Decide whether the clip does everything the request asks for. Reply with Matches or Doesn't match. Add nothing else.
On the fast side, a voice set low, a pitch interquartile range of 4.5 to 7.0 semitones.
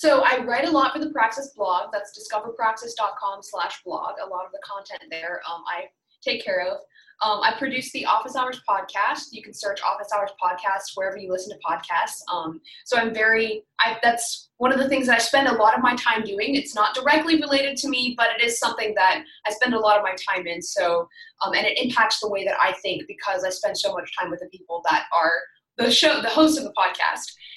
Doesn't match